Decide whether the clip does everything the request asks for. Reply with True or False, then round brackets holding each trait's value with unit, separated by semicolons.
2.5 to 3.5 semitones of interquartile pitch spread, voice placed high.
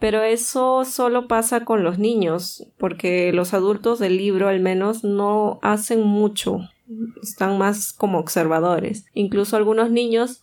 True (3.0 semitones; 210 Hz)